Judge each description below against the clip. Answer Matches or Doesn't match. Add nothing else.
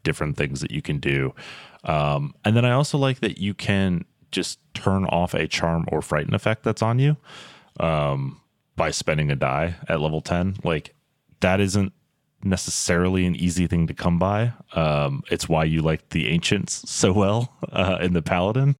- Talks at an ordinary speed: Matches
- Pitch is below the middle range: Matches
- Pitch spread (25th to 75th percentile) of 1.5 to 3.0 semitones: Doesn't match